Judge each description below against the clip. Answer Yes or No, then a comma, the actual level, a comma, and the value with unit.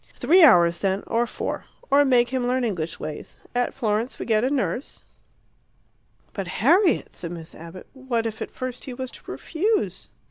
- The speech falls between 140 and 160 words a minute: No, average, 180 wpm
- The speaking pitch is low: No, high, 240 Hz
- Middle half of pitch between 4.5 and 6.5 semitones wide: Yes, wide, 5.5 semitones